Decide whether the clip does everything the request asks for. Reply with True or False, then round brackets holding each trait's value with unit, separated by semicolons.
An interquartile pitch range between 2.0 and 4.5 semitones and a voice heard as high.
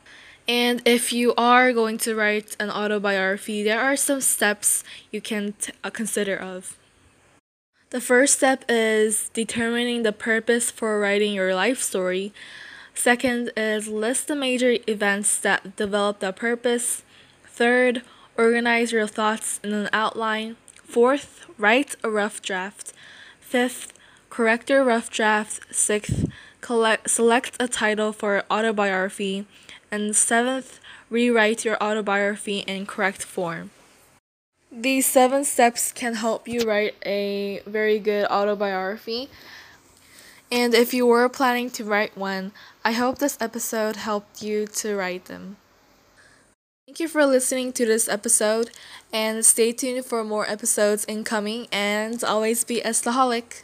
True (2.4 semitones; 220 Hz)